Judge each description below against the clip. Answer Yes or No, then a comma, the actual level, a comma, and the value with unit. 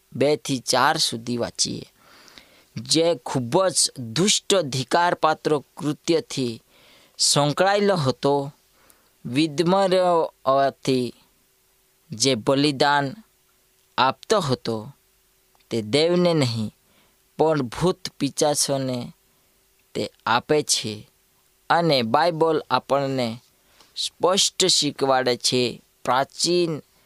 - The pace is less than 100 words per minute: Yes, average, 75 wpm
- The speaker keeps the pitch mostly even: No, average, 4.6 semitones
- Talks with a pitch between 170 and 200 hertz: No, medium, 140 Hz